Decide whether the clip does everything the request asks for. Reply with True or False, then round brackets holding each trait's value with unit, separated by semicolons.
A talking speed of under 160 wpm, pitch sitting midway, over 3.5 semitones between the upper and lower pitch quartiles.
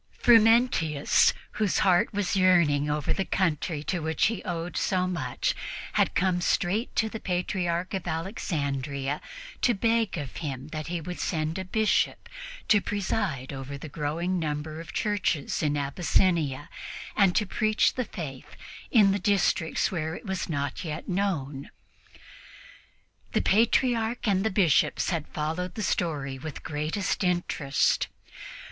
True (145 wpm; 175 Hz; 4.6 semitones)